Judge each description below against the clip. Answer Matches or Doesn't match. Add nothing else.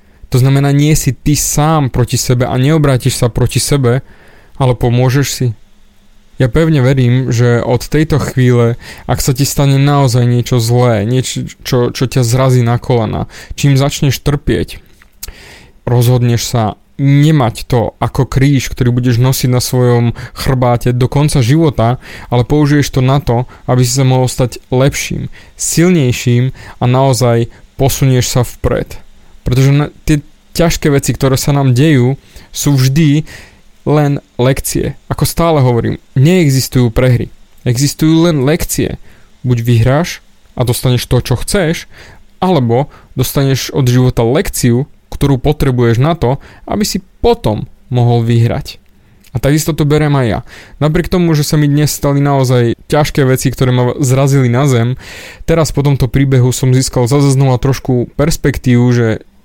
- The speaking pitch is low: Matches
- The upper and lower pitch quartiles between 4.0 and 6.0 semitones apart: Doesn't match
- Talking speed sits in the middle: Matches